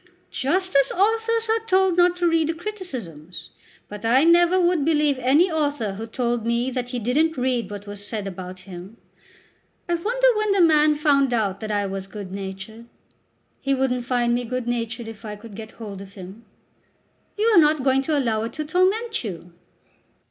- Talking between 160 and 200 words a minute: Yes, average, 190 wpm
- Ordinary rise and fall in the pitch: No, wide, 7.4 semitones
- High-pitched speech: Yes, very high, 255 Hz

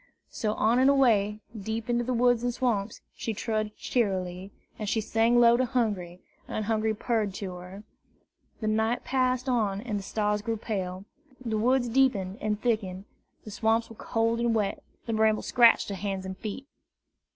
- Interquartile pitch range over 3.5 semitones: No, average, 2.7 semitones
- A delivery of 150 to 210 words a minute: Yes, average, 175 wpm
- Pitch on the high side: Yes, high, 220 Hz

